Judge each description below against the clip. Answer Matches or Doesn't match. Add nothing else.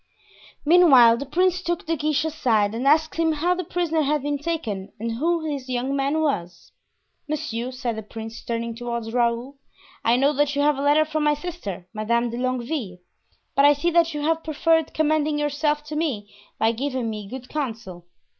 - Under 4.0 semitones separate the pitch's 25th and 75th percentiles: Doesn't match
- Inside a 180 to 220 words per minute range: Matches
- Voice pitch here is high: Matches